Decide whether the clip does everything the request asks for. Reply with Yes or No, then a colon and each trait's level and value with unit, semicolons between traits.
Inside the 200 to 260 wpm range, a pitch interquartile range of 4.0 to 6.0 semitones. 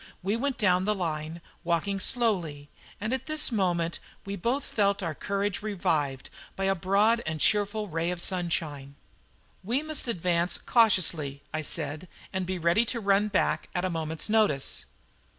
No: average, 160 wpm; average, 4.3 semitones